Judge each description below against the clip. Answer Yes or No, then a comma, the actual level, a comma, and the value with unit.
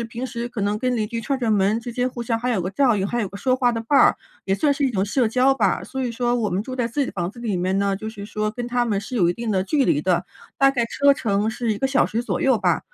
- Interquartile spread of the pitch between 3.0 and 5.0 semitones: Yes, average, 3.8 semitones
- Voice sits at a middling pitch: No, high, 230 Hz